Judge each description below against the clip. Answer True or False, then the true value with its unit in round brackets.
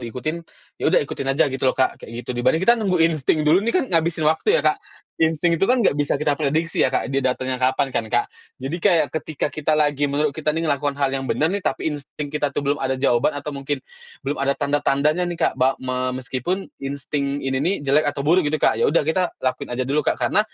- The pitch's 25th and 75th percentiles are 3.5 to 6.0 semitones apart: False (3.0 semitones)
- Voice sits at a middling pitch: True (145 Hz)